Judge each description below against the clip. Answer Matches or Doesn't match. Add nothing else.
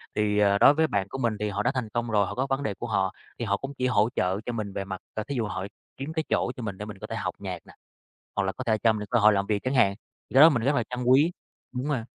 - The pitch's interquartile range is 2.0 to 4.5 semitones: Matches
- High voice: Doesn't match